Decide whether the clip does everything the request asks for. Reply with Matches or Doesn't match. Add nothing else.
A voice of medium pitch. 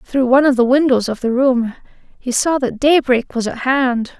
Doesn't match